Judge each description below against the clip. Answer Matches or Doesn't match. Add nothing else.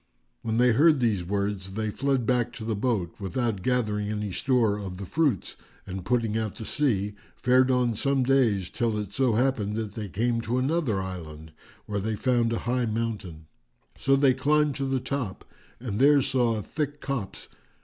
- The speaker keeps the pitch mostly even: Doesn't match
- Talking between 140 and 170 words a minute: Doesn't match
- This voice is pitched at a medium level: Doesn't match